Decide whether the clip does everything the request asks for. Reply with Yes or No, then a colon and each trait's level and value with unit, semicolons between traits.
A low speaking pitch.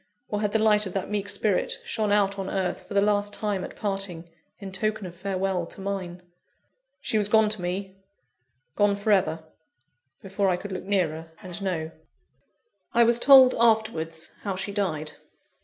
No: high, 200 Hz